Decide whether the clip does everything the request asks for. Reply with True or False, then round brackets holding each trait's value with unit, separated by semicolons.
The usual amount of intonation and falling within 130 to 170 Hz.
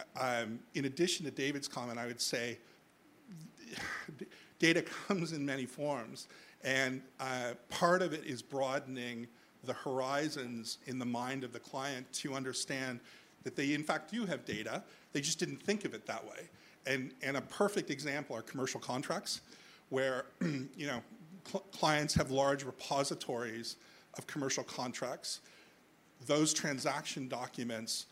True (3.0 semitones; 135 Hz)